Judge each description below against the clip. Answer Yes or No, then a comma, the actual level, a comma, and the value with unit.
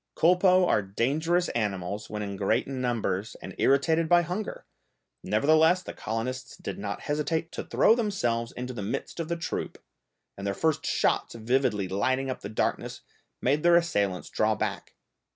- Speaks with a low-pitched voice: Yes, low, 130 Hz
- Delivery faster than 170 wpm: No, average, 160 wpm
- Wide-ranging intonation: Yes, wide, 7.8 semitones